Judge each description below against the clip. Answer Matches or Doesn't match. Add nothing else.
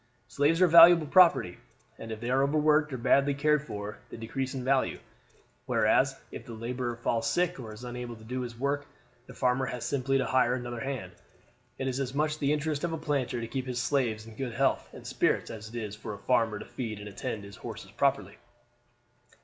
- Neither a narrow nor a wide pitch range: Matches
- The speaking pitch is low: Matches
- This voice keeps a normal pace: Doesn't match